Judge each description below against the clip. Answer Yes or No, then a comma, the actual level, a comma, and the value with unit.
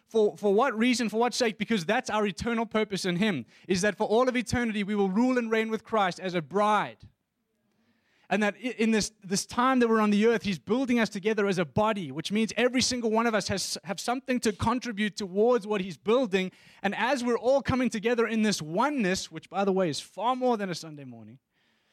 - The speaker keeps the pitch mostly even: No, average, 3.0 semitones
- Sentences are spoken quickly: Yes, fast, 230 wpm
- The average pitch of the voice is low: No, high, 215 Hz